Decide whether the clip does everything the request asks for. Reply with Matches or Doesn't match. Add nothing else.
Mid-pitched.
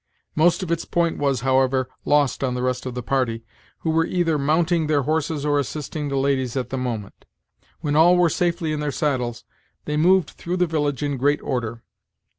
Matches